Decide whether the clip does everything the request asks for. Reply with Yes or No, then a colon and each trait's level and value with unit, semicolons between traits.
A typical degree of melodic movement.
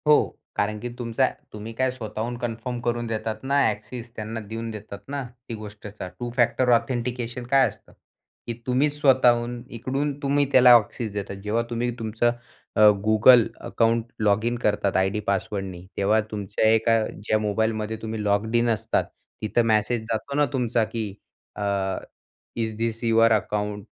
No: narrow, 2.2 semitones